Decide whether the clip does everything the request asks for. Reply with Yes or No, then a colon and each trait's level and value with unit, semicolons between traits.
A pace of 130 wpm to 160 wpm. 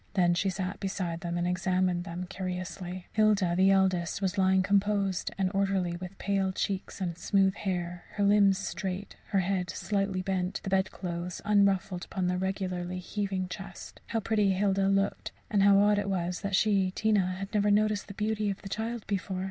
No: average, 180 wpm